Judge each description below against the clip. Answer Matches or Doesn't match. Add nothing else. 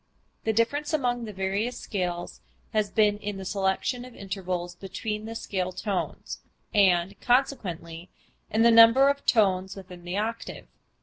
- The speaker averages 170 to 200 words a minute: Doesn't match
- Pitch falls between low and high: Doesn't match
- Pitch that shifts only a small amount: Doesn't match